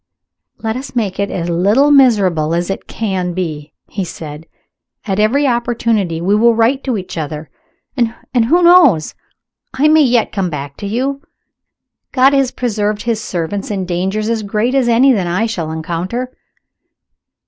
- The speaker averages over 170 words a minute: No, average, 160 wpm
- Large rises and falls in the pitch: Yes, wide, 5.7 semitones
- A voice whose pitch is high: Yes, high, 215 Hz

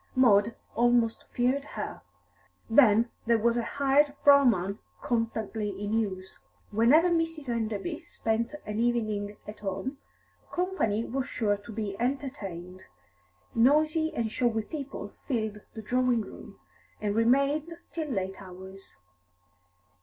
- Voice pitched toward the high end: Yes, high, 230 Hz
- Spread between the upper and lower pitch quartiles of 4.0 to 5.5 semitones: Yes, average, 4.6 semitones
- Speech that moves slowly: Yes, slow, 120 wpm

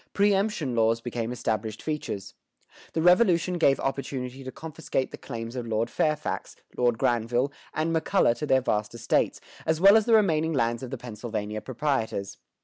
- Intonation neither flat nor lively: No, wide, 5.7 semitones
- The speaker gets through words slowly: No, average, 160 wpm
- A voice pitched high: No, low, 130 Hz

